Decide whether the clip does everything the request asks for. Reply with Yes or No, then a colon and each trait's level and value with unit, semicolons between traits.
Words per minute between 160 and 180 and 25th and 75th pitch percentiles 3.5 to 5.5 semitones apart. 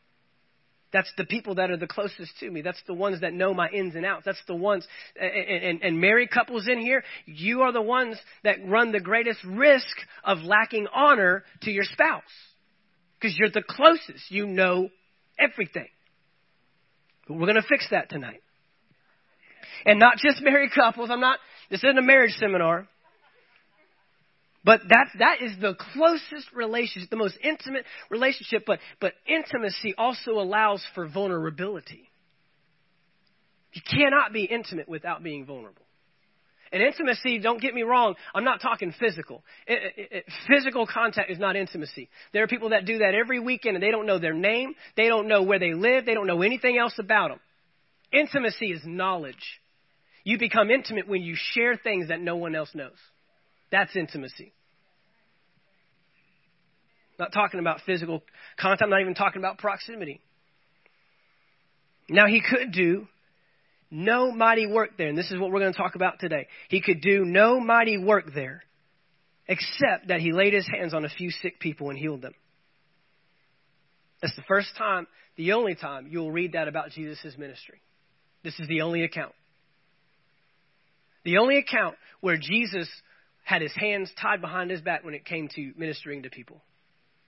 Yes: average, 165 wpm; average, 4.9 semitones